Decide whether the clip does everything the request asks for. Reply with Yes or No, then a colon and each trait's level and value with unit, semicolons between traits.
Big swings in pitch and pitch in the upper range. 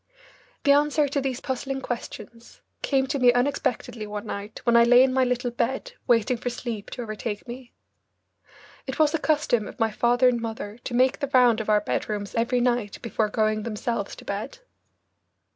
No: average, 2.9 semitones; high, 240 Hz